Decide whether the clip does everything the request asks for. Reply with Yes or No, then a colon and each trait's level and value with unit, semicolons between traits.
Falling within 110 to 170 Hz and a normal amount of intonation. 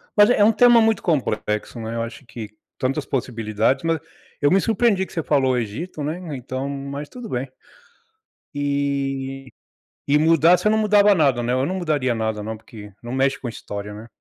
No: low, 135 Hz; wide, 5.8 semitones